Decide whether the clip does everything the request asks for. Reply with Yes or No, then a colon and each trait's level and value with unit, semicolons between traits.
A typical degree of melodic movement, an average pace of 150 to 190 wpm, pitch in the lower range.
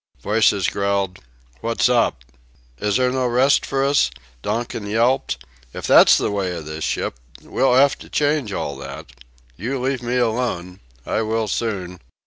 Yes: average, 4.4 semitones; average, 155 wpm; low, 115 Hz